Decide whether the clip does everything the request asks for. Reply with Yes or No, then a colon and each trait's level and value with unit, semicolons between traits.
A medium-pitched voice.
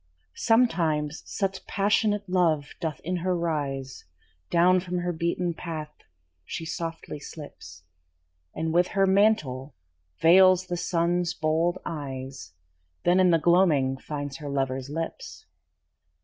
Yes: medium, 165 Hz